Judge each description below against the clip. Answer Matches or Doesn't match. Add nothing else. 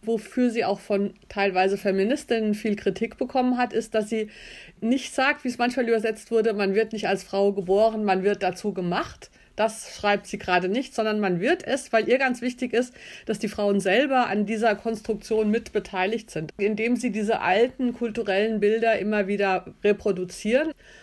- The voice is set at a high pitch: Matches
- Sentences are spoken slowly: Doesn't match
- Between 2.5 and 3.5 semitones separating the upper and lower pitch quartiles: Matches